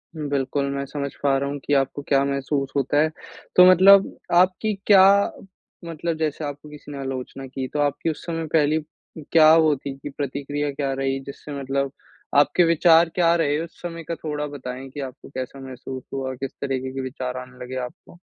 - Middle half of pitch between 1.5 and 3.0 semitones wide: Yes, average, 2.7 semitones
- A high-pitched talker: No, medium, 140 Hz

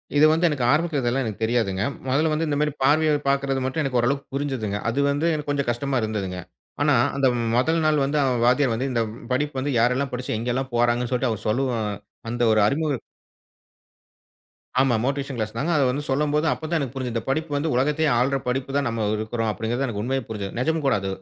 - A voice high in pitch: No, low, 135 Hz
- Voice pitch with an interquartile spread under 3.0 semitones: No, average, 3.4 semitones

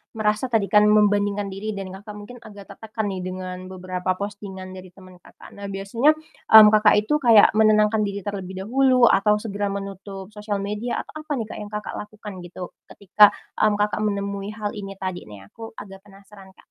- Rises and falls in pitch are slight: Yes, narrow, 1.7 semitones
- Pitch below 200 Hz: No, high, 205 Hz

